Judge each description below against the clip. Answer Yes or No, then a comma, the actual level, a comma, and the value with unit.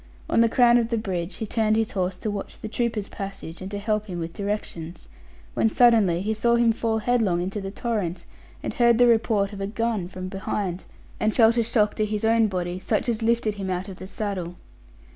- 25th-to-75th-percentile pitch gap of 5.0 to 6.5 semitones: No, average, 3.2 semitones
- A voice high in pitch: Yes, high, 210 Hz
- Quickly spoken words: Yes, fast, 220 wpm